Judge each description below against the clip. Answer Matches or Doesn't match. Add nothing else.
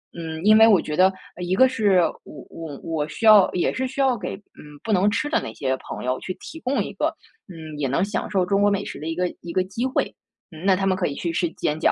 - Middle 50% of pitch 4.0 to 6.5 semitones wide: Matches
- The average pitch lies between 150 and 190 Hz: Matches